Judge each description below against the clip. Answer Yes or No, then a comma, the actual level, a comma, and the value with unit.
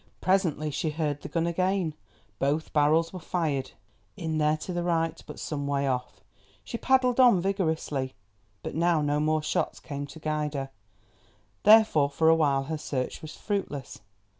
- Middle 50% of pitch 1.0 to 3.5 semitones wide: Yes, average, 3.1 semitones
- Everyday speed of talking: Yes, average, 165 wpm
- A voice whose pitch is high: No, medium, 155 Hz